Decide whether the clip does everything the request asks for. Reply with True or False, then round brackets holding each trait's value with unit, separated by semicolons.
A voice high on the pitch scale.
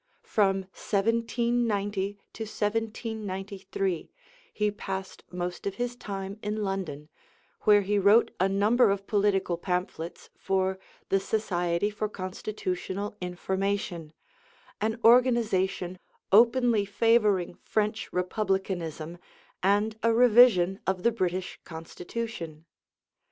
True (200 Hz)